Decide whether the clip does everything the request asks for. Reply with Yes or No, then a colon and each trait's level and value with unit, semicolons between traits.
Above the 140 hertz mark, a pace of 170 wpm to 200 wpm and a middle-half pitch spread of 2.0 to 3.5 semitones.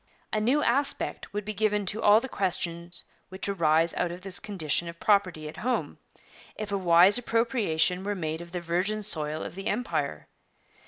No: high, 190 Hz; average, 180 wpm; average, 3.9 semitones